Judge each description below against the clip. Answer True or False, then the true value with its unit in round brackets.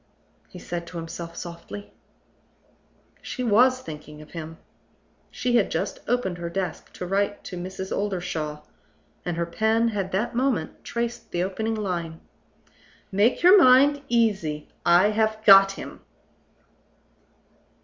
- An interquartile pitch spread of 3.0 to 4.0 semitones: False (4.8 semitones)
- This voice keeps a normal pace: False (130 wpm)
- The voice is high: True (195 Hz)